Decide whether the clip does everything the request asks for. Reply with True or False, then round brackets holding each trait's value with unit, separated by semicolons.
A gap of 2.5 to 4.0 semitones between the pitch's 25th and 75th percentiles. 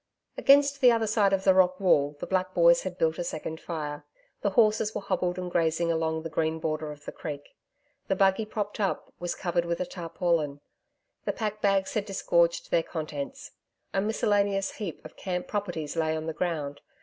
True (3.7 semitones)